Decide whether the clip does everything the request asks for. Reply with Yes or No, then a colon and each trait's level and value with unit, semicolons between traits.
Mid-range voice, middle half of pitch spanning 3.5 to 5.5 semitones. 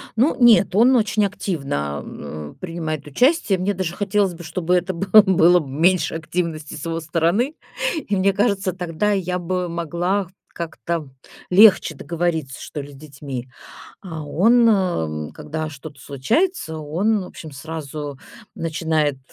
Yes: medium, 170 Hz; average, 4.2 semitones